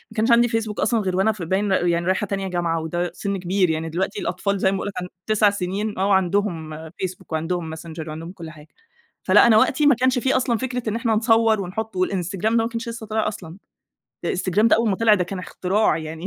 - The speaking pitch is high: Yes, high, 195 Hz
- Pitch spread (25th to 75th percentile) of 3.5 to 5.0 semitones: Yes, average, 4.0 semitones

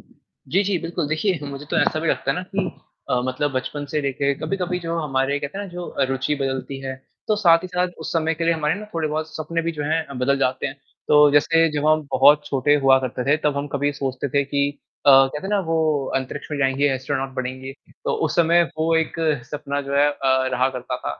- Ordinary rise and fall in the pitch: Yes, average, 3.3 semitones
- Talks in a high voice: No, medium, 145 Hz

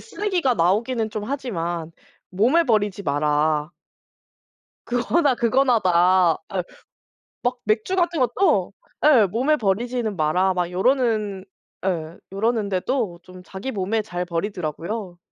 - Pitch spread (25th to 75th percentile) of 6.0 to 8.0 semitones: No, wide, 5.5 semitones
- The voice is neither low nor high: No, high, 205 Hz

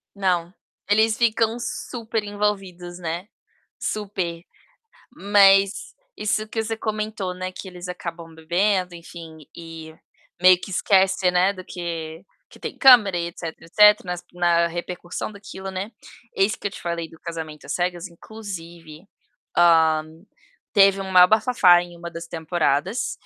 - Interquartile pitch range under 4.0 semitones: Yes, average, 3.2 semitones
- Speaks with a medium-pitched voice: Yes, medium, 180 Hz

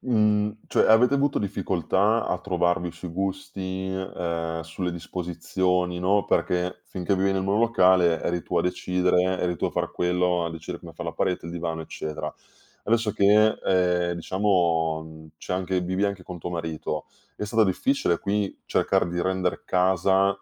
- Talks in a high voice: No, very low, 90 Hz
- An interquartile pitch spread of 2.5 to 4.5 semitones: No, narrow, 2.1 semitones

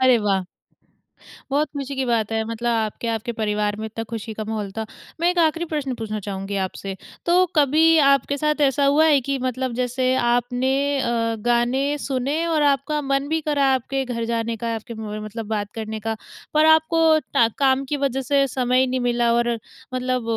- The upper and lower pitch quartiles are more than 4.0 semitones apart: No, average, 3.6 semitones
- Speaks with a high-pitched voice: Yes, high, 245 Hz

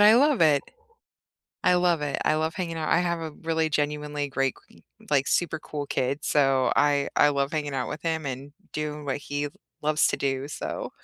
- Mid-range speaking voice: Yes, medium, 150 Hz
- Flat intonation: Yes, narrow, 2.3 semitones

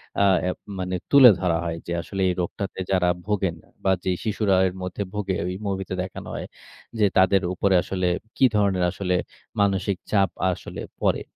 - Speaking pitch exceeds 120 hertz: No, very low, 95 Hz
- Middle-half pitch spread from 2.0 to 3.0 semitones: No, narrow, 1.6 semitones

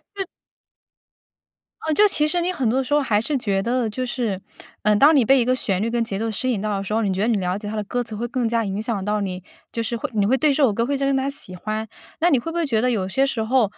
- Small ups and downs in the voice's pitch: No, average, 4.2 semitones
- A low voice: No, high, 230 Hz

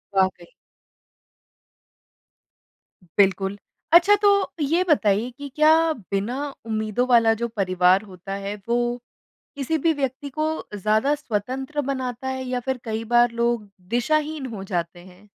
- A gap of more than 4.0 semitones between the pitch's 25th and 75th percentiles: Yes, average, 5.2 semitones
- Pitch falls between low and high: No, high, 235 Hz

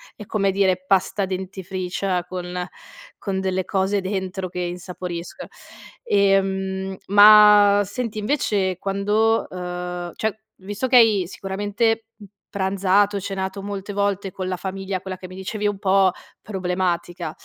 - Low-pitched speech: No, high, 195 Hz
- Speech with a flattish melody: Yes, narrow, 1.6 semitones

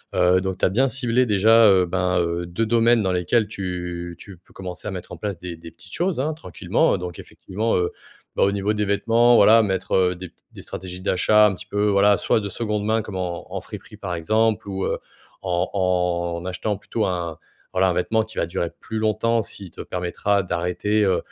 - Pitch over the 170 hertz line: No, very low, 95 Hz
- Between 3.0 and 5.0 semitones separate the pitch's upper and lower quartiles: Yes, average, 3.3 semitones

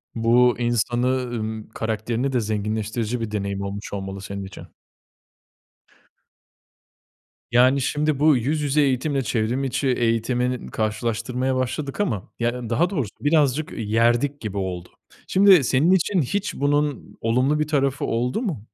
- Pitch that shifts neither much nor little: Yes, average, 4.3 semitones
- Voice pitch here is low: Yes, low, 125 Hz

